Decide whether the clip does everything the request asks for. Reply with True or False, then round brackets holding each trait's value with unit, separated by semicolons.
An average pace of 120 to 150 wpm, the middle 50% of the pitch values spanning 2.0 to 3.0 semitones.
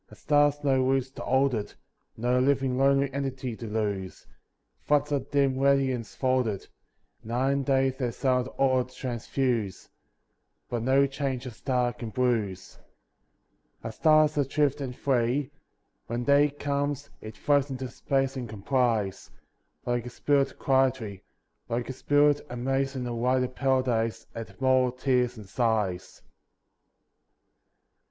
True (145 wpm; 2.5 semitones)